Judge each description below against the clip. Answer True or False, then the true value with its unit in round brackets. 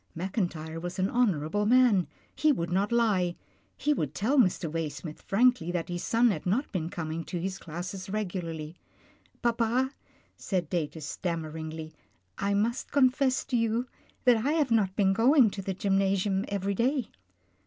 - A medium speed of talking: True (170 wpm)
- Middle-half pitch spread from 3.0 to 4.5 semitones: False (5.5 semitones)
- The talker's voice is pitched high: True (195 Hz)